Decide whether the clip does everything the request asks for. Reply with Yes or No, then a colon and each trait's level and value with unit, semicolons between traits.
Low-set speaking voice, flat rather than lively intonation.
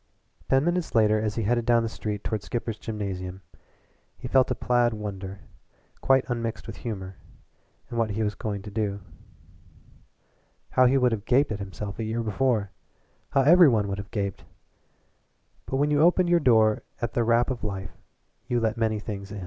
No: low, 110 Hz; average, 3.2 semitones